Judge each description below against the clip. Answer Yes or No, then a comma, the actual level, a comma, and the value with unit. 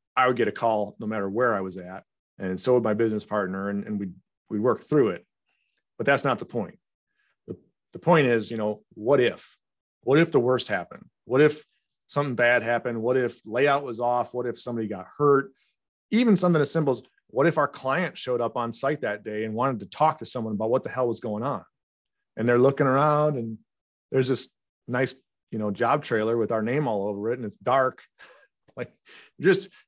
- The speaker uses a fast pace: Yes, fast, 215 wpm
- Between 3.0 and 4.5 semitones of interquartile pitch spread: Yes, average, 4.0 semitones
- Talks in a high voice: No, low, 120 Hz